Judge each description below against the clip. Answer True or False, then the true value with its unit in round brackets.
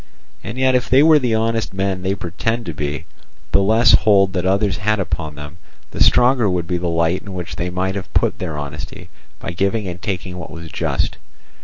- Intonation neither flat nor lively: True (4.1 semitones)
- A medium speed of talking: False (210 wpm)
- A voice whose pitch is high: False (95 Hz)